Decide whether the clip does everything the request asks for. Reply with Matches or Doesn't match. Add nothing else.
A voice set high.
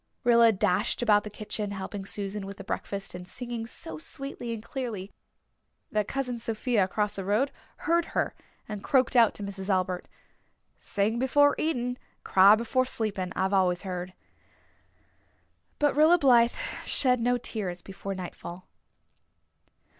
Matches